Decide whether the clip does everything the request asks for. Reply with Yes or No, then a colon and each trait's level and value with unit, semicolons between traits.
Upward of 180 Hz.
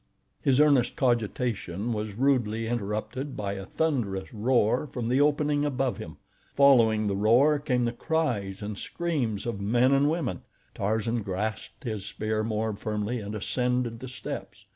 No: low, 115 Hz